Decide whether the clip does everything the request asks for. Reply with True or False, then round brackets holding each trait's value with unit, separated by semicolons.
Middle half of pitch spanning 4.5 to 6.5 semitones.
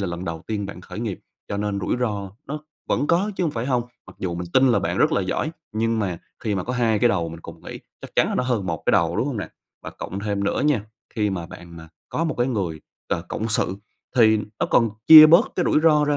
True (5.1 semitones)